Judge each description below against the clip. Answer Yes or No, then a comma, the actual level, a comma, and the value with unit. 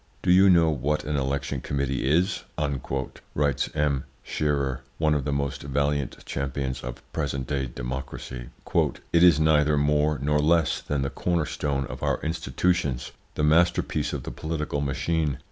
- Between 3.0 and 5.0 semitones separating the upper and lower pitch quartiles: No, narrow, 2.4 semitones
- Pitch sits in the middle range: No, very low, 70 Hz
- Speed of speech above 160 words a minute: No, average, 155 wpm